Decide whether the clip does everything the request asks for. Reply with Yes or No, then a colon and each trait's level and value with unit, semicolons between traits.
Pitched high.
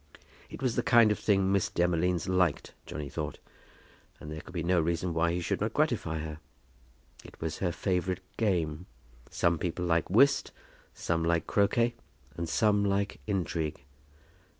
No: very low, 90 Hz